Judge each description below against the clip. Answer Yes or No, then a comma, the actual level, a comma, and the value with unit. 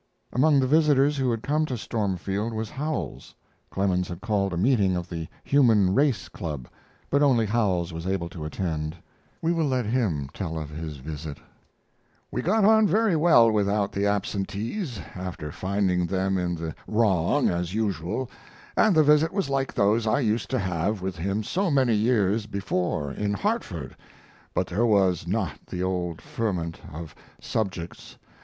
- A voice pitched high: No, low, 100 Hz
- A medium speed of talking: Yes, average, 165 wpm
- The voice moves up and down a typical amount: No, wide, 6.4 semitones